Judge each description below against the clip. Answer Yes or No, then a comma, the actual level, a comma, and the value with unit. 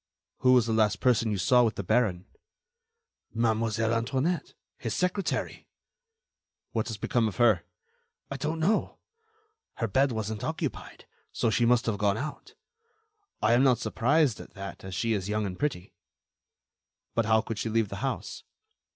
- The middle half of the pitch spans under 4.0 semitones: Yes, average, 3.0 semitones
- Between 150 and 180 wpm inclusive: Yes, average, 160 wpm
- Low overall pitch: Yes, low, 115 Hz